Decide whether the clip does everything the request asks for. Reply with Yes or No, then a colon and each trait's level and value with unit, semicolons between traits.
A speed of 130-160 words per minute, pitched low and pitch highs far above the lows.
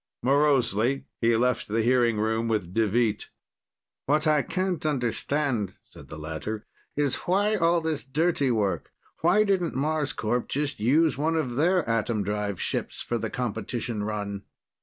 Yes: average, 145 wpm; low, 125 Hz; wide, 5.8 semitones